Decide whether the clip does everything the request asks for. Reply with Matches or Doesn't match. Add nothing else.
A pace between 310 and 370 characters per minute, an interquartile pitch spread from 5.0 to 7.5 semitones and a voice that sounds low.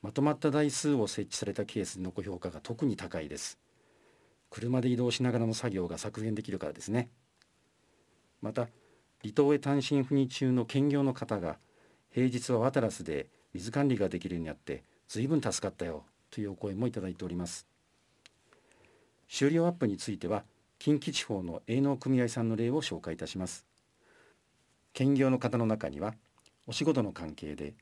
Matches